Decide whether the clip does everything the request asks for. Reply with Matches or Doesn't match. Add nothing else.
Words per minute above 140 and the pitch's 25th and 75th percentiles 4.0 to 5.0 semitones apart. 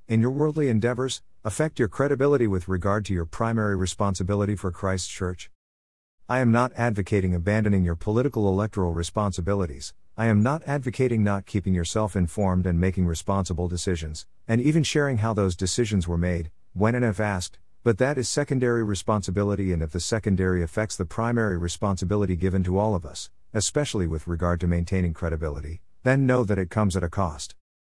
Matches